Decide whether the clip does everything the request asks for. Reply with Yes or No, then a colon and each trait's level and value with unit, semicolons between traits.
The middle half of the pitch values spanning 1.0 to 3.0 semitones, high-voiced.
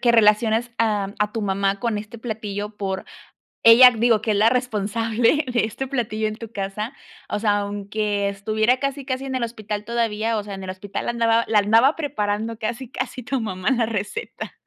Yes: narrow, 2.5 semitones; high, 220 Hz